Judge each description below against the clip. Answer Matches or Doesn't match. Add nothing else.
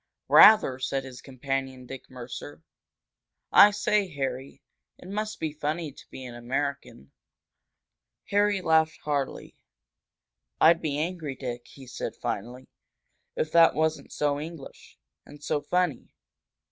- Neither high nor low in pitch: Matches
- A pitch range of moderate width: Matches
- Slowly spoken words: Matches